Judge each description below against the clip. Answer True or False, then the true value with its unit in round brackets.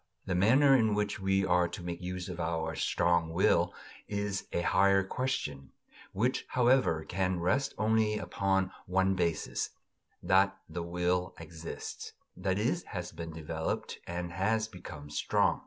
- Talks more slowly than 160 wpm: True (145 wpm)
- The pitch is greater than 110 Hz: False (90 Hz)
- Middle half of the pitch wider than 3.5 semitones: False (3.2 semitones)